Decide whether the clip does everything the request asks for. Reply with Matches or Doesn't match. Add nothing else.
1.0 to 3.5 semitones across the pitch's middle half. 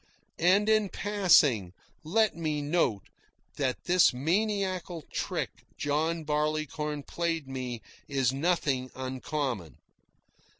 Doesn't match